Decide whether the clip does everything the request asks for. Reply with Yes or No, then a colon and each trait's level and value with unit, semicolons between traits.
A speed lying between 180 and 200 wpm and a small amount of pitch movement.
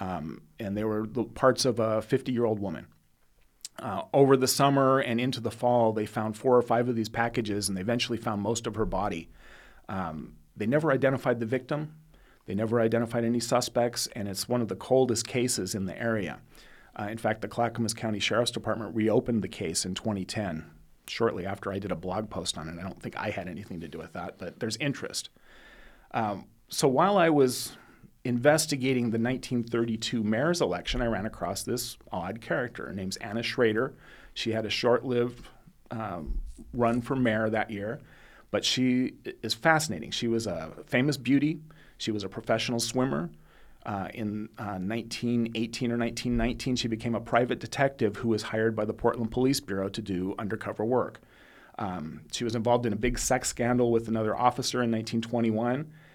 Yes: average, 185 wpm; narrow, 2.3 semitones